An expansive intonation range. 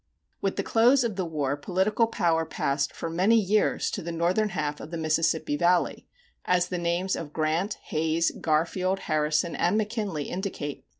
No: average, 3.6 semitones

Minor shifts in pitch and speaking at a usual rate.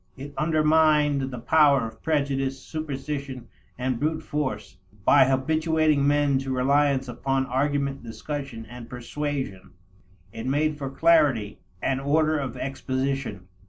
No: narrow, 2.3 semitones; slow, 125 wpm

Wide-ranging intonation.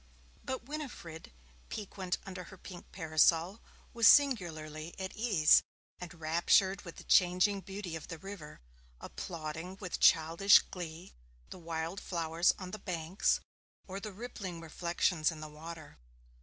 No: average, 3.2 semitones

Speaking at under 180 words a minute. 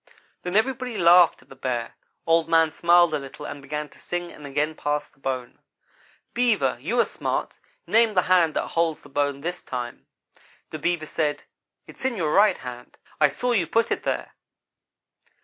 No: average, 185 wpm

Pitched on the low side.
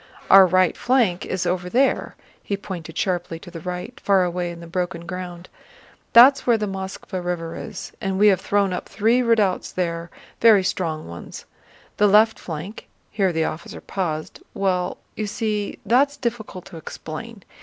No: medium, 185 Hz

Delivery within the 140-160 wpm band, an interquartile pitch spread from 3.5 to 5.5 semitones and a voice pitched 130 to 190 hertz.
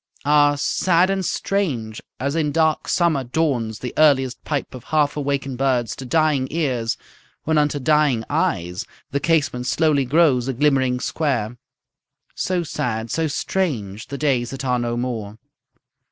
Yes: average, 150 wpm; average, 4.0 semitones; medium, 140 Hz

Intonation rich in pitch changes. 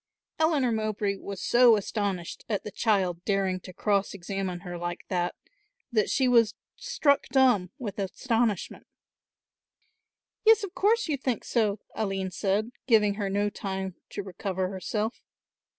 No: average, 3.7 semitones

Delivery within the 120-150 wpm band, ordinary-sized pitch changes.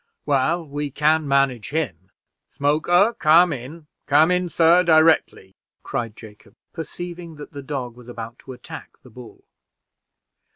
Yes: slow, 135 wpm; average, 4.7 semitones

